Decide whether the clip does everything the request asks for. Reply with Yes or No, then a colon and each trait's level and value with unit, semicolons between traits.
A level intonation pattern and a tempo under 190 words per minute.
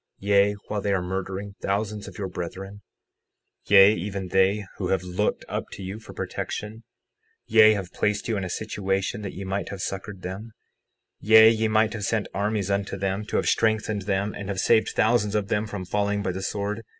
No: narrow, 1.7 semitones; average, 200 wpm